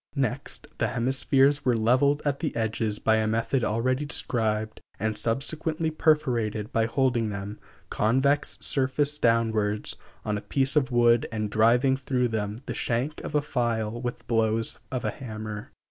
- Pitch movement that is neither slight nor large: Yes, average, 3.7 semitones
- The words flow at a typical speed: Yes, average, 155 wpm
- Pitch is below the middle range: Yes, low, 120 Hz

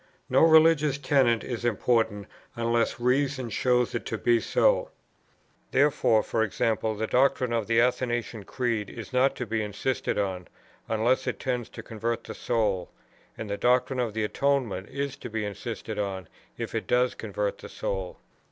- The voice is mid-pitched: No, low, 115 Hz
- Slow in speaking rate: No, average, 160 wpm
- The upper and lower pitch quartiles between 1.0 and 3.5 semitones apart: Yes, average, 2.9 semitones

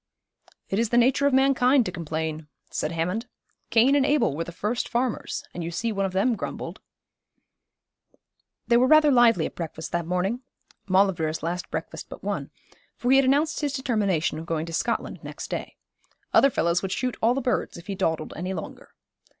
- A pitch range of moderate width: No, wide, 6.9 semitones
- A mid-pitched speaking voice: No, high, 200 Hz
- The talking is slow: No, average, 190 wpm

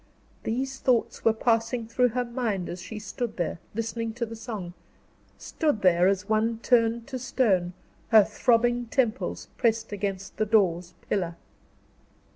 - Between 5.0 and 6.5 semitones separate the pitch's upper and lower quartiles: No, average, 3.3 semitones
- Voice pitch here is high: Yes, high, 225 Hz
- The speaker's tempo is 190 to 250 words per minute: No, average, 145 wpm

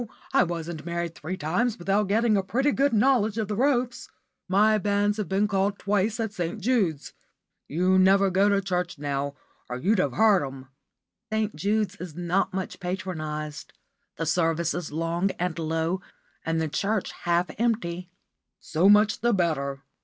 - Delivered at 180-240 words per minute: No, average, 165 wpm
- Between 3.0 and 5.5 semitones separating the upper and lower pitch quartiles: Yes, average, 4.0 semitones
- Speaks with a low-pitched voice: No, medium, 185 Hz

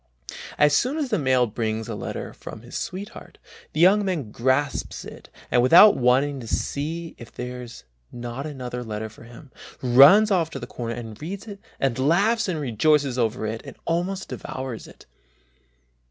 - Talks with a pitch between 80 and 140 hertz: Yes, low, 135 Hz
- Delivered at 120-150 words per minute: No, average, 170 wpm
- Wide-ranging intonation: Yes, wide, 5.8 semitones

